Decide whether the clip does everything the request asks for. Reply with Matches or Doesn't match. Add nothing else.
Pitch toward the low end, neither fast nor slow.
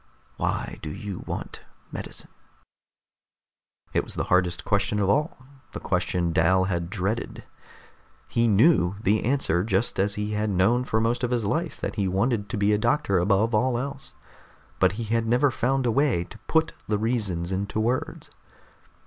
Matches